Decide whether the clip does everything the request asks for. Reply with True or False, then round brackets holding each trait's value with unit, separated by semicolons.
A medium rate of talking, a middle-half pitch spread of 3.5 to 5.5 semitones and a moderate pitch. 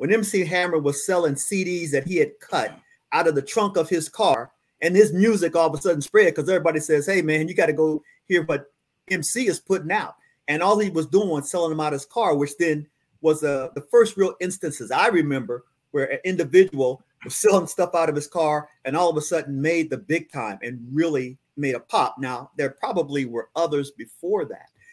False (225 wpm; 4.7 semitones; 165 Hz)